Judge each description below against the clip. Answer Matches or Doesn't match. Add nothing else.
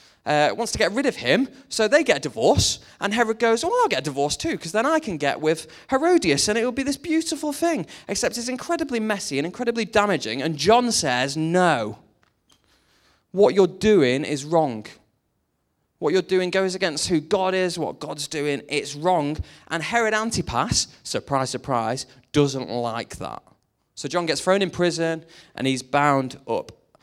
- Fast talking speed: Doesn't match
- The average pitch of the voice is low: Doesn't match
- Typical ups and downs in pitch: Doesn't match